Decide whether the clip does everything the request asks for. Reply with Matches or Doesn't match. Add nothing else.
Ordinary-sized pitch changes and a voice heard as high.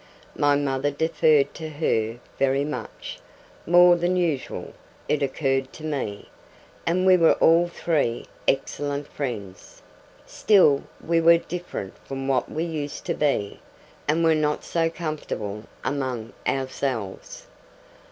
Doesn't match